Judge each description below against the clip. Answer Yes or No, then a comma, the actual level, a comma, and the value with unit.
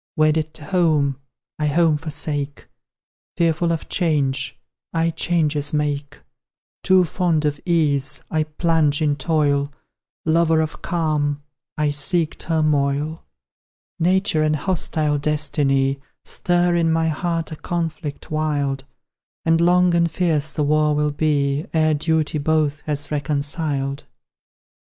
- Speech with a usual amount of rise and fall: No, narrow, 2.1 semitones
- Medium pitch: Yes, medium, 155 Hz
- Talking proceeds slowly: Yes, slow, 120 wpm